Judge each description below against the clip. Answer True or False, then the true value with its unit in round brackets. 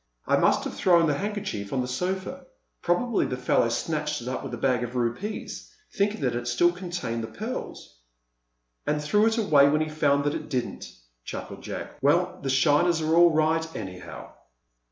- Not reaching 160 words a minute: False (185 wpm)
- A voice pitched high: False (150 Hz)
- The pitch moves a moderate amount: False (5.7 semitones)